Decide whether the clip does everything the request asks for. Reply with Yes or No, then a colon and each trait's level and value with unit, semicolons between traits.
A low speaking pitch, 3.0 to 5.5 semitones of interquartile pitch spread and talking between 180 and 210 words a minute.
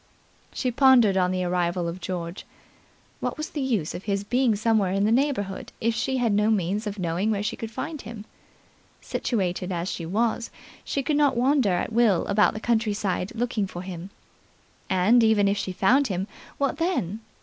No: high, 210 Hz; average, 4.3 semitones; average, 185 wpm